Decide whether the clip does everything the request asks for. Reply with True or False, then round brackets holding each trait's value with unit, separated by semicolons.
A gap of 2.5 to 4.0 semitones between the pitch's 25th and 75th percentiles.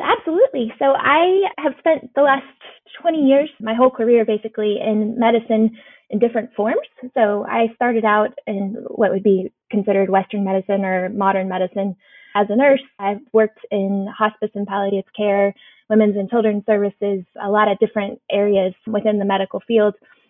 True (3.0 semitones)